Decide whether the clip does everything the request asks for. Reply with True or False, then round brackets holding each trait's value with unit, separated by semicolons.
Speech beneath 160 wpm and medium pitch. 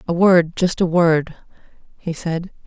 True (135 wpm; 170 Hz)